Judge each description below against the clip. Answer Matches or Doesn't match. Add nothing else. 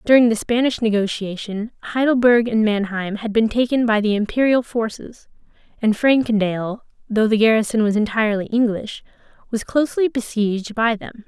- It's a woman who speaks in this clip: Matches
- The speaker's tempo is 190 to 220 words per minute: Doesn't match